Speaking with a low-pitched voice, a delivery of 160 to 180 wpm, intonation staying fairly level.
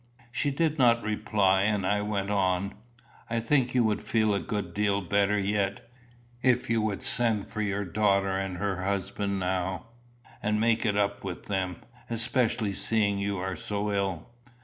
Yes: low, 100 Hz; average, 170 wpm; narrow, 2.1 semitones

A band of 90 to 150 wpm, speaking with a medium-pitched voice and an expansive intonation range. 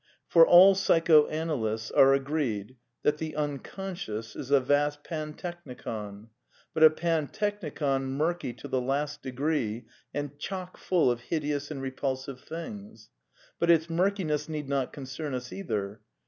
No: average, 140 wpm; medium, 145 Hz; average, 3.8 semitones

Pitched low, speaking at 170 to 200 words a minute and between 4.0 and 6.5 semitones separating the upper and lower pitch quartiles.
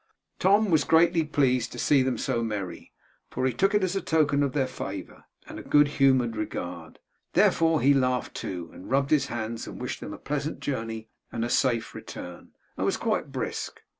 Yes: low, 130 Hz; average, 190 wpm; average, 4.8 semitones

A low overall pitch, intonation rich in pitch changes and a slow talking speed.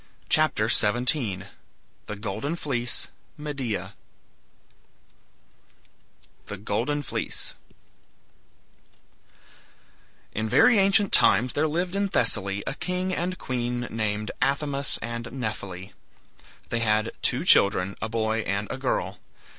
Yes: low, 120 Hz; wide, 5.7 semitones; slow, 105 wpm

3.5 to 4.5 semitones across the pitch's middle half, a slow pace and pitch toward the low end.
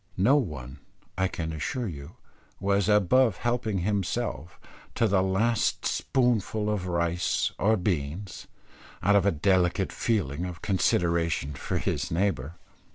Yes: average, 4.0 semitones; slow, 130 wpm; very low, 95 Hz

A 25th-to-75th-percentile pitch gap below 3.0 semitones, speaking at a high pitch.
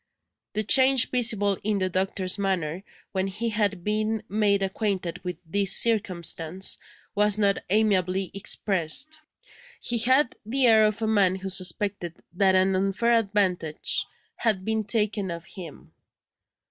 Yes: narrow, 2.6 semitones; high, 200 Hz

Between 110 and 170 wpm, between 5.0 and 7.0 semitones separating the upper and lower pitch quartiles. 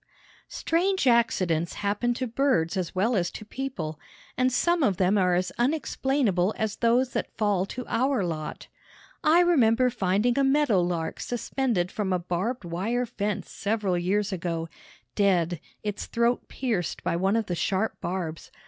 Yes: average, 155 wpm; wide, 5.5 semitones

